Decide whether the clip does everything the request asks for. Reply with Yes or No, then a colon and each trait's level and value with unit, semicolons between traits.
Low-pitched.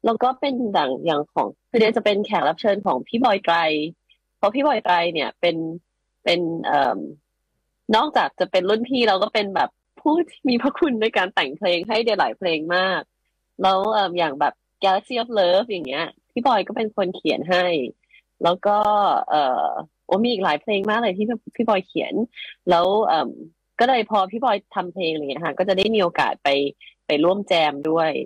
No: high, 195 Hz